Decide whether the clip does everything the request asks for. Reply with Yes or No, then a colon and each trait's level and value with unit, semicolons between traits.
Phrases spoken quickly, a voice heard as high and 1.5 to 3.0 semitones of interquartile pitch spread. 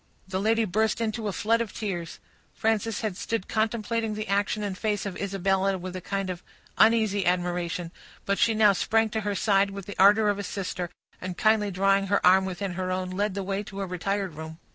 Yes: fast, 210 wpm; high, 200 Hz; narrow, 2.6 semitones